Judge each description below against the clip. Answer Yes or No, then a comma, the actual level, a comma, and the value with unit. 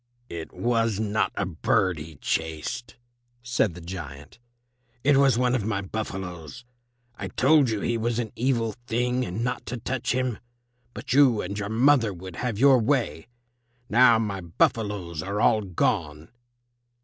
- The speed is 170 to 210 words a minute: No, average, 155 wpm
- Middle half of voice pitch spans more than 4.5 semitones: Yes, average, 5.1 semitones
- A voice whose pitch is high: No, low, 110 Hz